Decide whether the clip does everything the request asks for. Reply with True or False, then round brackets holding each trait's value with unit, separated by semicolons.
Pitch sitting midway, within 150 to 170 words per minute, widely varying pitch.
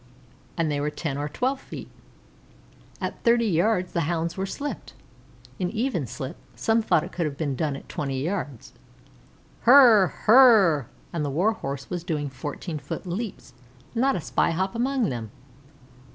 True (170 Hz; 160 wpm; 7.2 semitones)